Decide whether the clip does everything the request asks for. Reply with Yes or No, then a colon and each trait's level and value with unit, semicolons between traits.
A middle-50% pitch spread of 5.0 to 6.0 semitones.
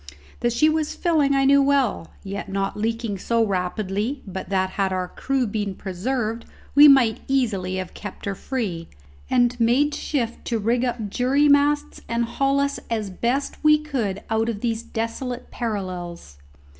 Yes: wide, 5.4 semitones